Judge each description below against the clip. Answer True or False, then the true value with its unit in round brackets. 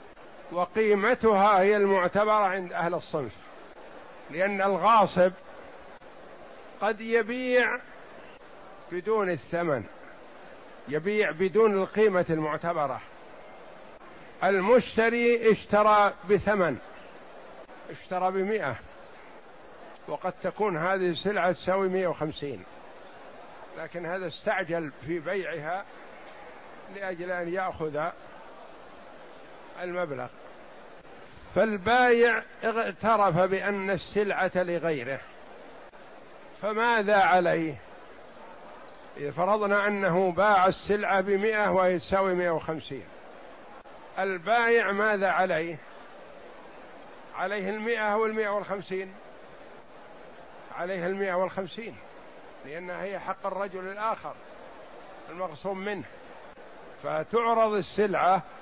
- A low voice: False (190 Hz)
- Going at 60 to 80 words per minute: True (75 wpm)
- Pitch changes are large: False (2.9 semitones)